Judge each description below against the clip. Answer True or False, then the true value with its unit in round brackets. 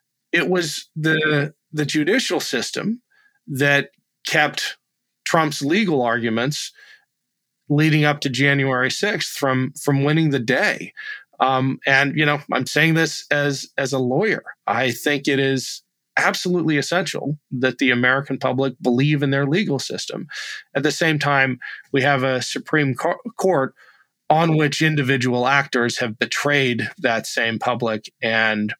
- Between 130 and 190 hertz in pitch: True (140 Hz)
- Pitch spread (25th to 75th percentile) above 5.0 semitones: False (2.9 semitones)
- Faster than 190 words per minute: False (140 wpm)